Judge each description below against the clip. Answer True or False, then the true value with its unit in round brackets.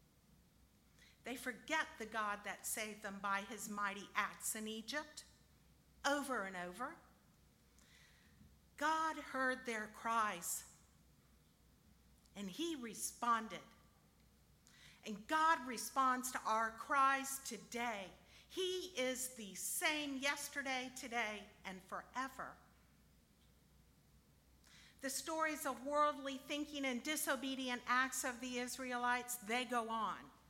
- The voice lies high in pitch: True (245 Hz)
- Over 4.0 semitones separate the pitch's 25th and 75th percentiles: True (4.6 semitones)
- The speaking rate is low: True (100 wpm)